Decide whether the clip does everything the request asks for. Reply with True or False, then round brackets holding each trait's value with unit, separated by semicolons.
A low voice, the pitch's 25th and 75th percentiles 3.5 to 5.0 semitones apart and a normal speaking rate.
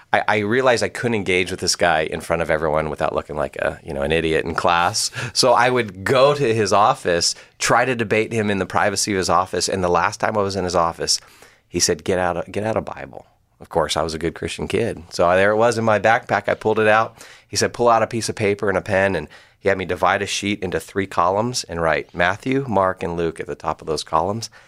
False (100 Hz; 4.1 semitones; 270 wpm)